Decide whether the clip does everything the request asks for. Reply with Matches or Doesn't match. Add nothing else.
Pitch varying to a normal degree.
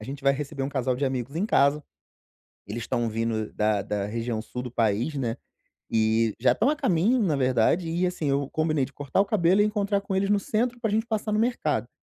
Doesn't match